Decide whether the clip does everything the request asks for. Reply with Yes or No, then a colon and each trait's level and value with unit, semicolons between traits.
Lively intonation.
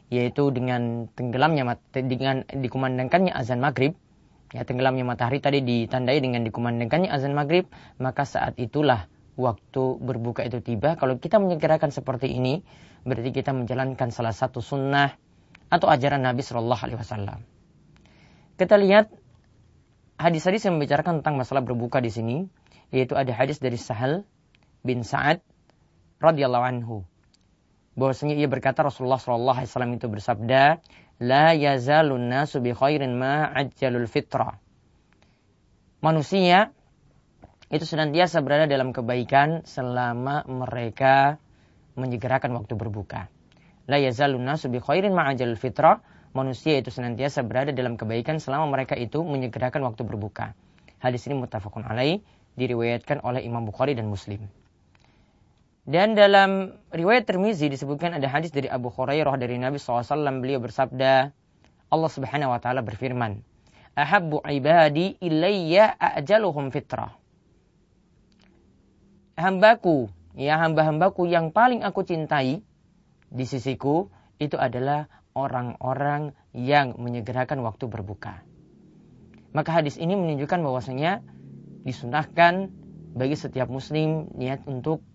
No: average, 3.7 semitones